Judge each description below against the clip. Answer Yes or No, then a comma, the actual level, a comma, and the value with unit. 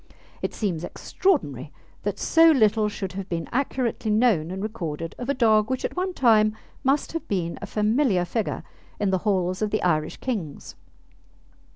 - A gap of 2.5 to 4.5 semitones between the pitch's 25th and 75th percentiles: No, average, 5.3 semitones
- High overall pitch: Yes, high, 210 Hz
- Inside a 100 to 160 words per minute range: No, average, 170 wpm